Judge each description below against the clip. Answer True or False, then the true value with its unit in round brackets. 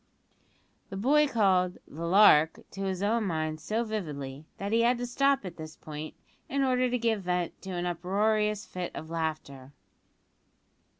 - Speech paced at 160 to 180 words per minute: True (165 wpm)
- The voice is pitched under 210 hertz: True (190 Hz)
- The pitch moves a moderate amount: False (5.8 semitones)